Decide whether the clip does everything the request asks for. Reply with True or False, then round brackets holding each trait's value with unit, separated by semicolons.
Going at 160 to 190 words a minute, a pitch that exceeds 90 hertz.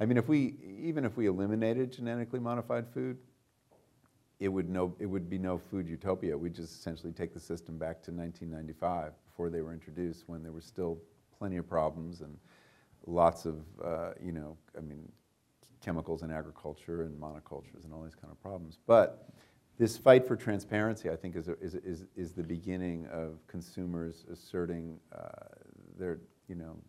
False (175 wpm; 85 Hz)